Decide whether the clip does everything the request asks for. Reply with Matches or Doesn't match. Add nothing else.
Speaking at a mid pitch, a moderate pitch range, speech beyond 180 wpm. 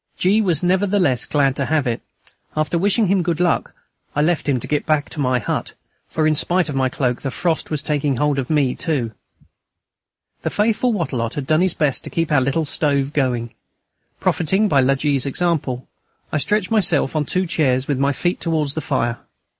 Matches